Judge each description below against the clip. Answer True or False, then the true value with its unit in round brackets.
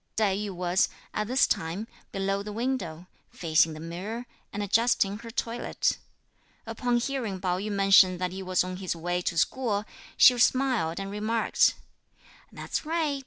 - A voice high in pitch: True (200 Hz)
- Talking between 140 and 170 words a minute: True (160 wpm)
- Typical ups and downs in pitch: True (4.2 semitones)